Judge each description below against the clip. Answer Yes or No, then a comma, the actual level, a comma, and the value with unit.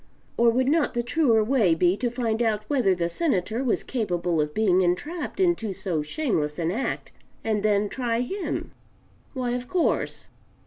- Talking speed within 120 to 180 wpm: Yes, average, 170 wpm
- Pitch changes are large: Yes, wide, 5.9 semitones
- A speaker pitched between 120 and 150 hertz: No, high, 225 Hz